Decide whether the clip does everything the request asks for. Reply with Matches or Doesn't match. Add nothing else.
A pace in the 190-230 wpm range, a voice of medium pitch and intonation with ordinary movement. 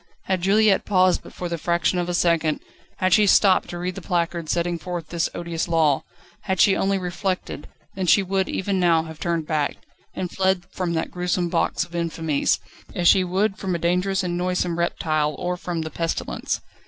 Doesn't match